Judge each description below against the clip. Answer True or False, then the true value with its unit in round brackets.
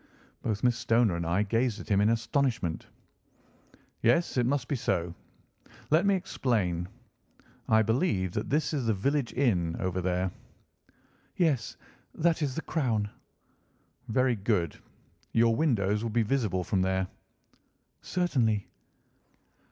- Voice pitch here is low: True (115 Hz)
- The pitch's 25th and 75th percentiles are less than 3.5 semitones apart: False (5.5 semitones)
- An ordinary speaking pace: False (130 wpm)